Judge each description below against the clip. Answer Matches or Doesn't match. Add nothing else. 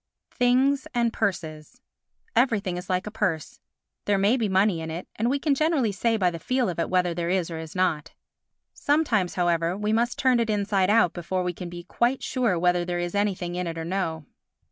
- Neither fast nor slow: Doesn't match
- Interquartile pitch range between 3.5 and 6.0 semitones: Matches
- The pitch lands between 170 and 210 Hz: Matches